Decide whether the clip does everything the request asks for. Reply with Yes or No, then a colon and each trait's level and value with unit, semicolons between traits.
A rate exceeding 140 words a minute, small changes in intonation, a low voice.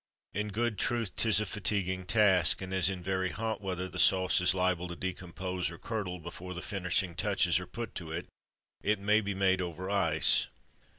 Yes: average, 190 wpm; narrow, 2.2 semitones; very low, 95 Hz